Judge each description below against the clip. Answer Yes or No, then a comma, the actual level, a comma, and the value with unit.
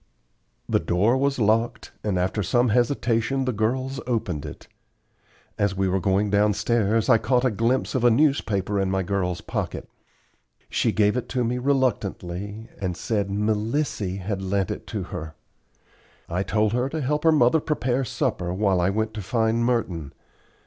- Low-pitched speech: Yes, low, 110 Hz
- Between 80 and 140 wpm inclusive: No, average, 165 wpm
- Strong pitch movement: No, average, 4.3 semitones